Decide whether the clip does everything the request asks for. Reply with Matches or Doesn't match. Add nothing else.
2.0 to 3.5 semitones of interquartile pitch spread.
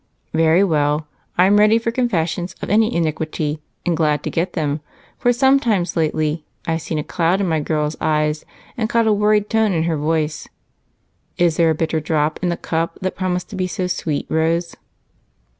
Doesn't match